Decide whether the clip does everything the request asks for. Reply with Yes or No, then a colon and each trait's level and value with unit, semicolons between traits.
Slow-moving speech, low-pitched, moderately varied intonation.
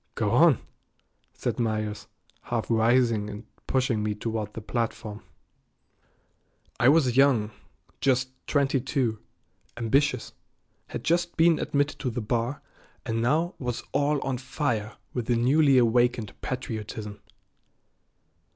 Yes: slow, 120 wpm; low, 120 Hz; average, 3.5 semitones